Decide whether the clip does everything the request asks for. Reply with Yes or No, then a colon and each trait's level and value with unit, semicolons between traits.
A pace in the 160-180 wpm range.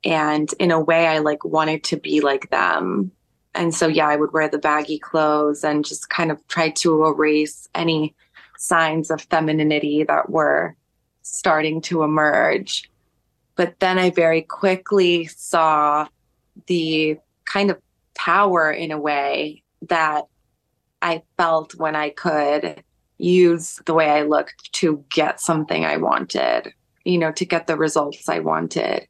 No: average, 150 wpm